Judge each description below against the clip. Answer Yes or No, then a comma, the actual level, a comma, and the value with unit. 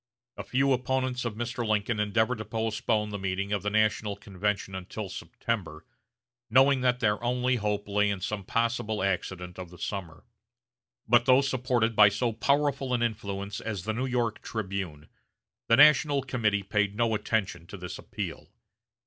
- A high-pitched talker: No, low, 110 Hz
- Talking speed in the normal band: Yes, average, 165 wpm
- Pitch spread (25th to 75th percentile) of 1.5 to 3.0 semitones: No, average, 3.5 semitones